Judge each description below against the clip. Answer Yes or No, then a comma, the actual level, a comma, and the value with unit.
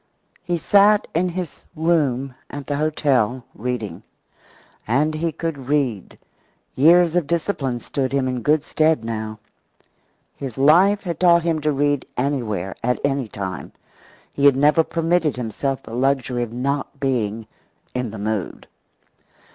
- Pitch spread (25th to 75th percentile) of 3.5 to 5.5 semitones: Yes, average, 4.5 semitones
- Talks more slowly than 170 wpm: Yes, average, 140 wpm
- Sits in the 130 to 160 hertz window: Yes, medium, 140 Hz